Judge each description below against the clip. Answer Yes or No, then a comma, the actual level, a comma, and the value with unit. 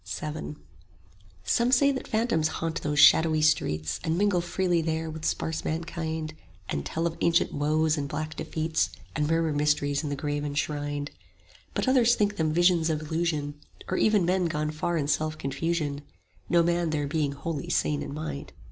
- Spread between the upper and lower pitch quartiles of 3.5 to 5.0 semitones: No, narrow, 2.5 semitones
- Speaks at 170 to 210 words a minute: Yes, average, 175 wpm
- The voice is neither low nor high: Yes, medium, 155 Hz